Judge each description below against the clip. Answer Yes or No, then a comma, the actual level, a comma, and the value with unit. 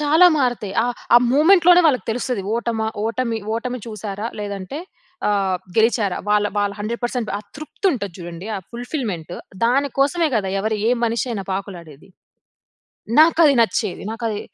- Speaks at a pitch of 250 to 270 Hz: No, high, 225 Hz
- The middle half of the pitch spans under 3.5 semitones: No, average, 4.1 semitones